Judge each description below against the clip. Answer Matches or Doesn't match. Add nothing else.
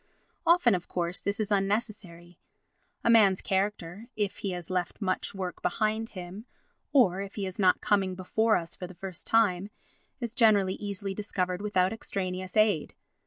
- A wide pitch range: Doesn't match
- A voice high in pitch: Matches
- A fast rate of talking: Doesn't match